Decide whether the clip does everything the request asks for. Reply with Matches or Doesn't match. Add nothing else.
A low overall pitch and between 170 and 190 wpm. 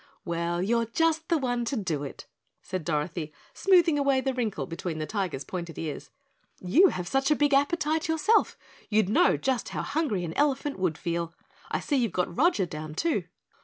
Doesn't match